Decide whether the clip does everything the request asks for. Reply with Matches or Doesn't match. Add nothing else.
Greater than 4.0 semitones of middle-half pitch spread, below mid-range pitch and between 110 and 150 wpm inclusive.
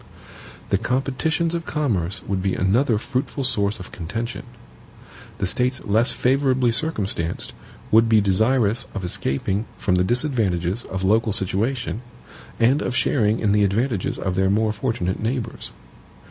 Matches